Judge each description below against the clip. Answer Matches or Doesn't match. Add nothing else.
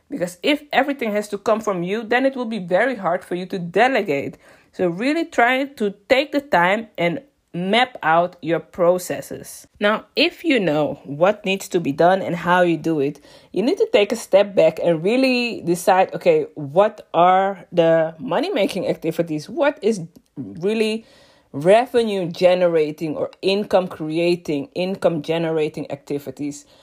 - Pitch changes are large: Matches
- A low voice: Doesn't match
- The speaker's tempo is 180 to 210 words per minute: Doesn't match